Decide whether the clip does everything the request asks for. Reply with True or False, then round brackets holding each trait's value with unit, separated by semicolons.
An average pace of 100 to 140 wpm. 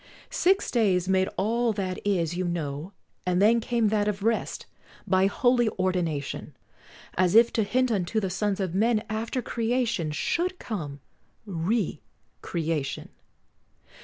True (135 wpm)